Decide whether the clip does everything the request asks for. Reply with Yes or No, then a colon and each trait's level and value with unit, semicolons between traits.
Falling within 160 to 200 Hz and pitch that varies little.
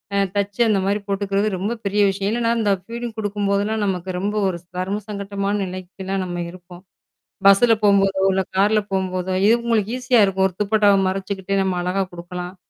Yes: high, 195 Hz; narrow, 1.7 semitones